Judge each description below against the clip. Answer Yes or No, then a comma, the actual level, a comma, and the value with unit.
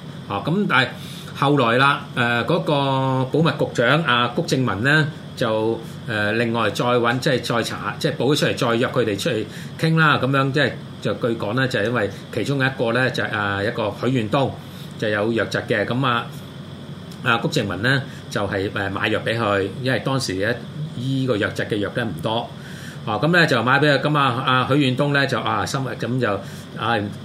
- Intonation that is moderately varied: Yes, average, 4.2 semitones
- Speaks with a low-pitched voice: Yes, low, 130 Hz